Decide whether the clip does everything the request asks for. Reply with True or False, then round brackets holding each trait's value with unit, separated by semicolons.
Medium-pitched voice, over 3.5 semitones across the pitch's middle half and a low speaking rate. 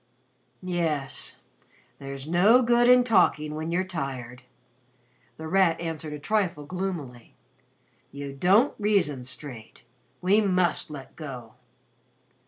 True (160 Hz; 5.5 semitones; 115 wpm)